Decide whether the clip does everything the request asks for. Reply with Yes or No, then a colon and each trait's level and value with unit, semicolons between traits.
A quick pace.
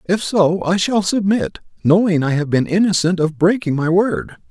No: average, 185 wpm